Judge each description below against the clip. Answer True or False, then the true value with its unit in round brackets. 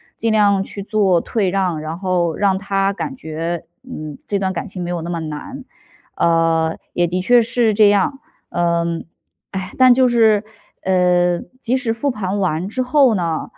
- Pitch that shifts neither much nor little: True (4.3 semitones)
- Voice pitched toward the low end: False (190 Hz)